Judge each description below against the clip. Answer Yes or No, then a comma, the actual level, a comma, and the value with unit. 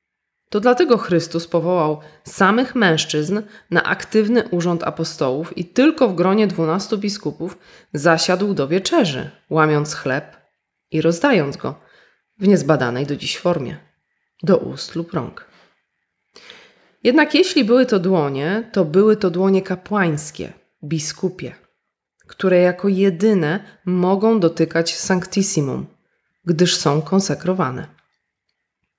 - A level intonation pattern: No, average, 4.1 semitones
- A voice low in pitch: No, medium, 180 Hz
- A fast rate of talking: No, slow, 110 wpm